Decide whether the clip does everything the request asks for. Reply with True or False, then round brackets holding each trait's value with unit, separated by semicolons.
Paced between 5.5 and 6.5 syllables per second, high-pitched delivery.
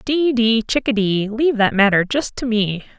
False (4.9 syllables/s; 225 Hz)